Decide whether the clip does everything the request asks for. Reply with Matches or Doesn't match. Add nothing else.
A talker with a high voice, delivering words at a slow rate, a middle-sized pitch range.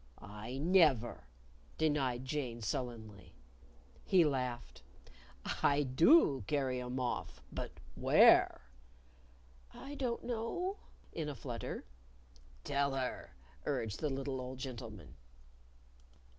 Doesn't match